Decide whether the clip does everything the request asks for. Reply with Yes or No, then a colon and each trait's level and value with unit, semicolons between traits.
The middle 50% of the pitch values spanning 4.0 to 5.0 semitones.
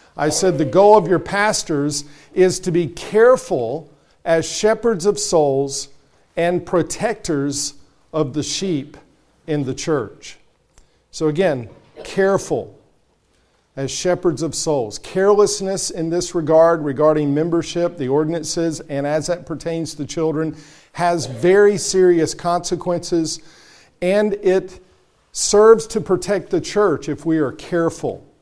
No: average, 3.5 semitones